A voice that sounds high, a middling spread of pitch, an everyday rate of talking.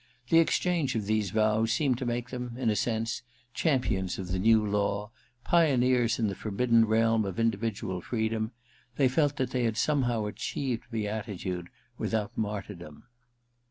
No: low, 115 Hz; average, 3.1 semitones; average, 160 wpm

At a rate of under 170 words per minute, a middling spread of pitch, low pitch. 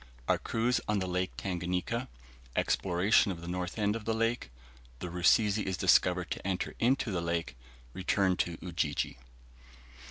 Yes: average, 155 wpm; average, 3.4 semitones; very low, 95 Hz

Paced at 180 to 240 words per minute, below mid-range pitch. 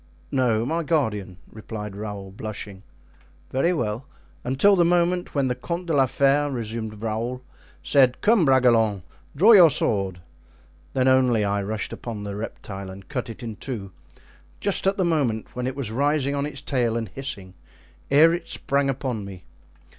No: average, 165 wpm; low, 125 Hz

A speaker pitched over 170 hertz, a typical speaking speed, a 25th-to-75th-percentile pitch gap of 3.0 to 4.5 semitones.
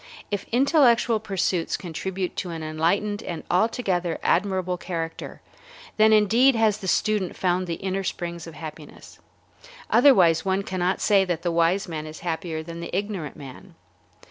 Yes: medium, 185 Hz; average, 150 wpm; average, 3.6 semitones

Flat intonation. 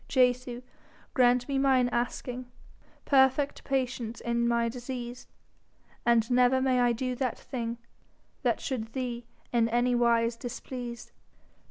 Yes: narrow, 1.4 semitones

